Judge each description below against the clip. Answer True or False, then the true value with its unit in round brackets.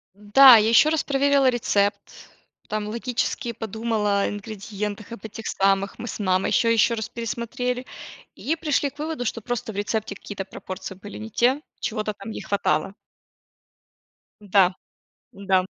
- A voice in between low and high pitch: False (220 Hz)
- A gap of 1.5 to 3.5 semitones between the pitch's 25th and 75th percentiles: True (3.2 semitones)